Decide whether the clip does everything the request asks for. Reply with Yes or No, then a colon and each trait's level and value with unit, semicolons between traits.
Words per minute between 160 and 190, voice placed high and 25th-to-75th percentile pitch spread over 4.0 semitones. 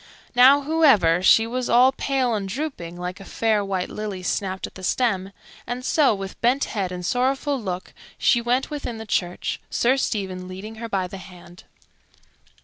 Yes: average, 175 wpm; high, 215 Hz; average, 5.3 semitones